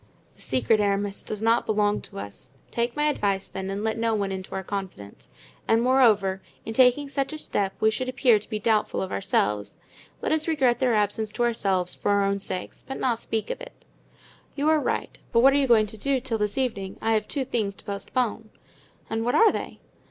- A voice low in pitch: No, high, 220 Hz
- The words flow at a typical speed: No, fast, 220 wpm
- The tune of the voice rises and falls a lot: No, average, 4.2 semitones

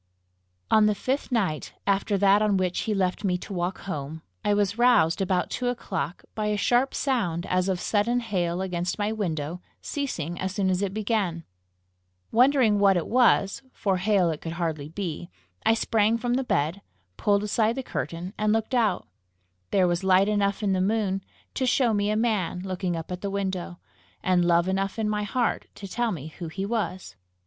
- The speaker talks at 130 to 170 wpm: No, average, 190 wpm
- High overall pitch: Yes, high, 195 Hz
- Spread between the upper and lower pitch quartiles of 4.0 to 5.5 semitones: No, average, 3.3 semitones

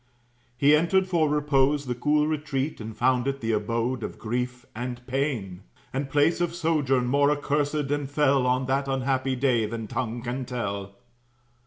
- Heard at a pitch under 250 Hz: Yes, low, 135 Hz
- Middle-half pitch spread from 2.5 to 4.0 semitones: Yes, average, 3.1 semitones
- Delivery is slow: No, average, 165 wpm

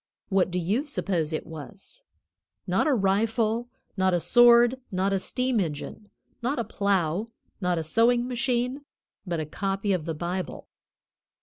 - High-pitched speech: Yes, high, 200 Hz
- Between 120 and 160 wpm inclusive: Yes, average, 150 wpm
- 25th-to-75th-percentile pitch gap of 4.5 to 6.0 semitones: Yes, average, 5.2 semitones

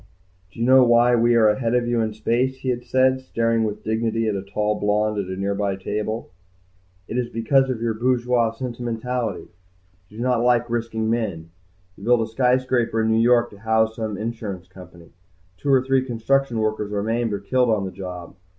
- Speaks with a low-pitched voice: Yes, low, 115 Hz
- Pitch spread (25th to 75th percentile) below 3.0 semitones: Yes, narrow, 2.5 semitones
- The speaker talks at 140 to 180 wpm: No, average, 200 wpm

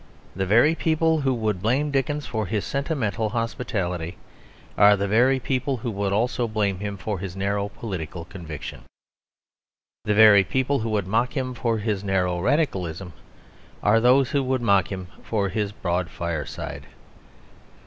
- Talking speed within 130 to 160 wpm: Yes, average, 155 wpm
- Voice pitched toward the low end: Yes, low, 105 Hz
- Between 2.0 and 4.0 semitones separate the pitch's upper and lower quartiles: No, average, 4.6 semitones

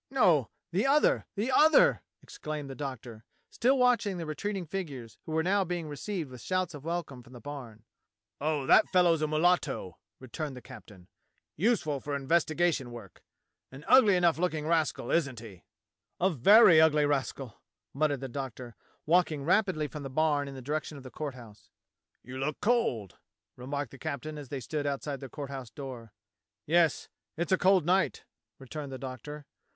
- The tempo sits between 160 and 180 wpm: Yes, average, 175 wpm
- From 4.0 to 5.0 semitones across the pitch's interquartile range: Yes, average, 4.7 semitones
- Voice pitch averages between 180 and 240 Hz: No, medium, 150 Hz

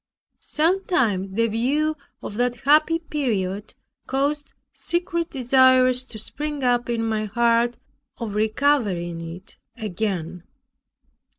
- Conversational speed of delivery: No, slow, 105 wpm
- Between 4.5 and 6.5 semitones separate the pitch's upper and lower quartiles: Yes, wide, 5.4 semitones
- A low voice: No, high, 240 Hz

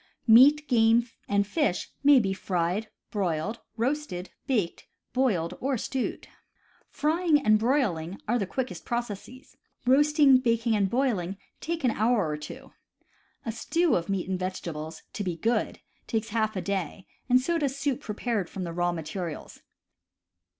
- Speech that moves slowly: No, average, 150 wpm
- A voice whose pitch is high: Yes, high, 225 Hz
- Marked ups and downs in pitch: Yes, wide, 5.8 semitones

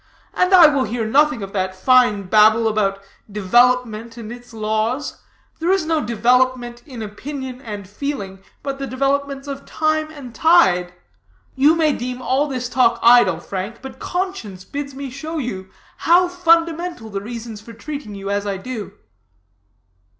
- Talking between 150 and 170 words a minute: Yes, average, 155 wpm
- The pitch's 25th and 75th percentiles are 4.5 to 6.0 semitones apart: Yes, average, 5.1 semitones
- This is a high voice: Yes, high, 245 Hz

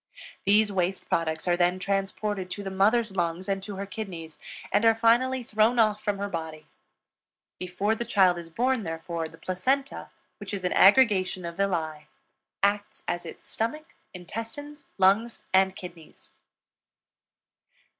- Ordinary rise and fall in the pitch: Yes, average, 3.7 semitones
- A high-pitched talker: Yes, high, 195 Hz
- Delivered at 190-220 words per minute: No, average, 145 wpm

